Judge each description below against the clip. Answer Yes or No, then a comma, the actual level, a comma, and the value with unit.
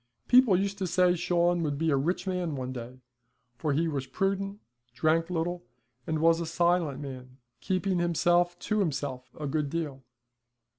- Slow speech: No, average, 165 wpm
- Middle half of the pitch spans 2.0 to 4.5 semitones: Yes, average, 3.9 semitones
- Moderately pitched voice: Yes, medium, 165 Hz